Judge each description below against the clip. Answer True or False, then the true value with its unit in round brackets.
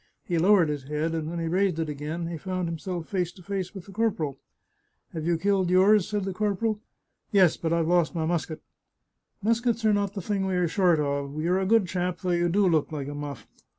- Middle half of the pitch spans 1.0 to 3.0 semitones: False (3.4 semitones)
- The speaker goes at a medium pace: False (245 wpm)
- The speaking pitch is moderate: True (175 Hz)